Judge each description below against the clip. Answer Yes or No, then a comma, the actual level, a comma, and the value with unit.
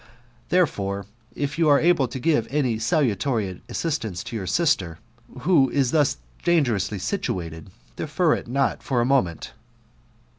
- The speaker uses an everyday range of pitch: No, wide, 7.2 semitones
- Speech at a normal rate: Yes, average, 145 wpm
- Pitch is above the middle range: No, low, 130 Hz